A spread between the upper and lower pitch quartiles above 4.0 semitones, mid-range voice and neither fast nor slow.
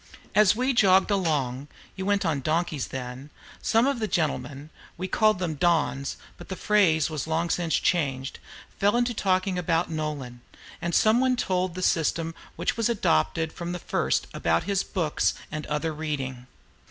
Yes: average, 4.4 semitones; medium, 170 Hz; average, 170 wpm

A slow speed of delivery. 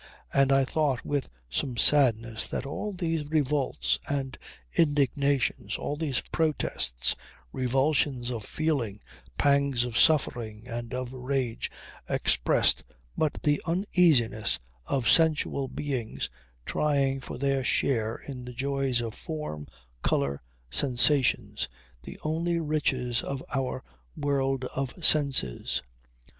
Yes: slow, 115 wpm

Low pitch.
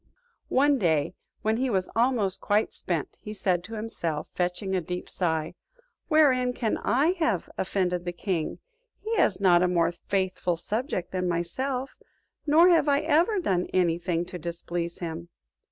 No: high, 190 Hz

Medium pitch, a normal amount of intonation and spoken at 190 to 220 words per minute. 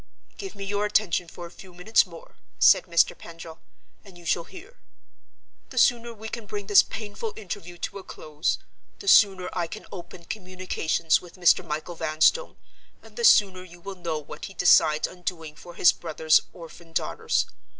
No: medium, 180 Hz; average, 3.5 semitones; average, 180 wpm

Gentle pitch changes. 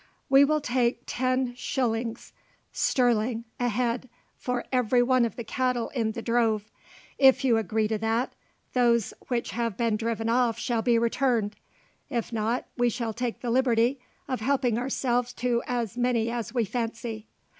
Yes: narrow, 1.7 semitones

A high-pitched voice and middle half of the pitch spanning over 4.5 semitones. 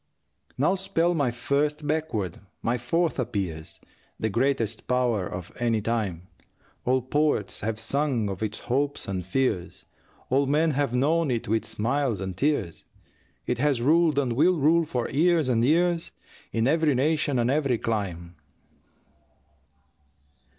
No: low, 125 Hz; average, 5.2 semitones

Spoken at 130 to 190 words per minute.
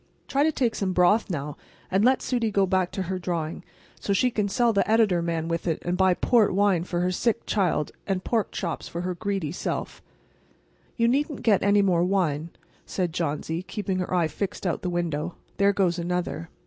No: average, 200 wpm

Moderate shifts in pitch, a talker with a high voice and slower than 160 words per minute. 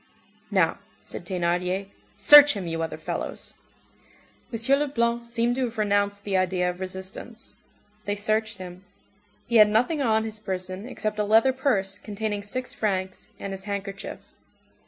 Yes: average, 3.4 semitones; high, 205 Hz; average, 150 wpm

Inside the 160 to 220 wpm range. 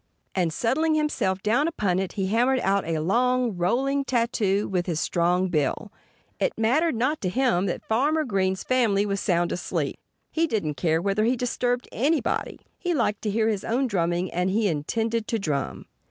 Yes: average, 180 wpm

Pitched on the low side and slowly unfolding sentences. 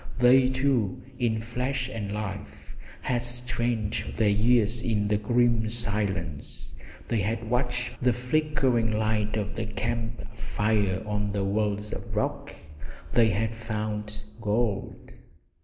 Yes: low, 110 Hz; slow, 130 wpm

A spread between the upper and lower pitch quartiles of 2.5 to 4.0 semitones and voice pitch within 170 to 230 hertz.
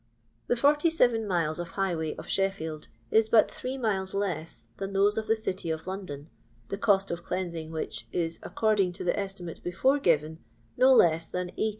No: average, 4.5 semitones; high, 190 Hz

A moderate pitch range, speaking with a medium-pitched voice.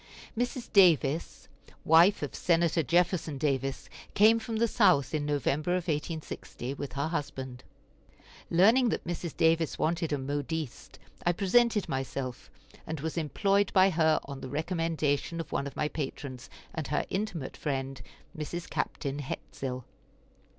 Yes: average, 4.0 semitones; medium, 160 Hz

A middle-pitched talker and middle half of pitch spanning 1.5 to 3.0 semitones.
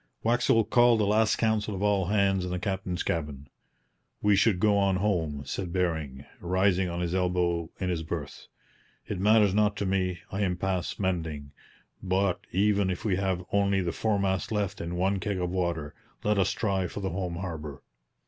No: very low, 95 Hz; narrow, 2.5 semitones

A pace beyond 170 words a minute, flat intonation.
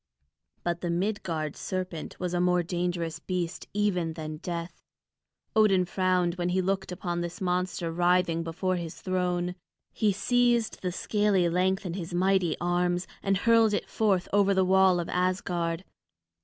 No: average, 155 wpm; narrow, 1.6 semitones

